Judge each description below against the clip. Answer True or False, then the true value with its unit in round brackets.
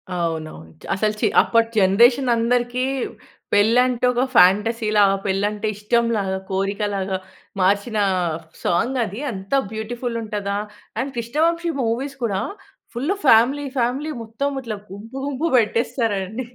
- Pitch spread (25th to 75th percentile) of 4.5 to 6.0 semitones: False (3.6 semitones)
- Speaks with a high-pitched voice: True (225 Hz)